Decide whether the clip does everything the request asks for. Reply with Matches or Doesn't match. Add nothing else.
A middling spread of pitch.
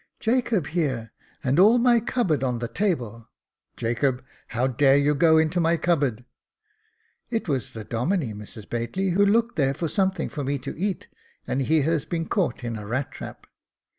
Doesn't match